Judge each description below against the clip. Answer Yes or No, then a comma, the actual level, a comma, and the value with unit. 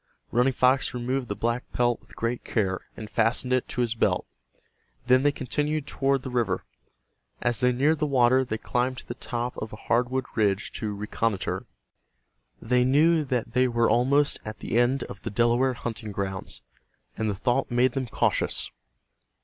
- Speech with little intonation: Yes, narrow, 2.3 semitones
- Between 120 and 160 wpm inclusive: No, average, 175 wpm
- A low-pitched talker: Yes, low, 120 Hz